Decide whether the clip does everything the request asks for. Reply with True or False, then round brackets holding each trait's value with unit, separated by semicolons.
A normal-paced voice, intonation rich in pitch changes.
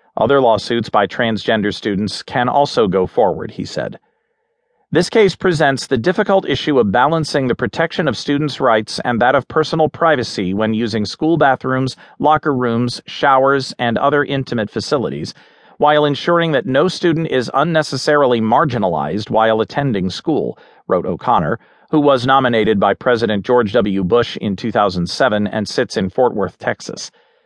True (150 wpm; 6.0 semitones)